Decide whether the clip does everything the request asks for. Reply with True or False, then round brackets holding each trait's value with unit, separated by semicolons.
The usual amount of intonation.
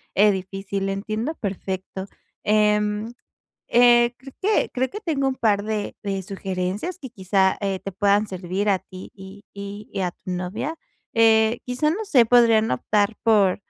True (3.4 semitones)